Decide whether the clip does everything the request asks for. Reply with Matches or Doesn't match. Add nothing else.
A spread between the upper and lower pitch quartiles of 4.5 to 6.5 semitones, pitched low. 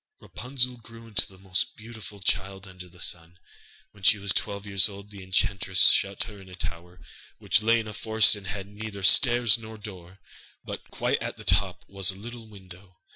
Doesn't match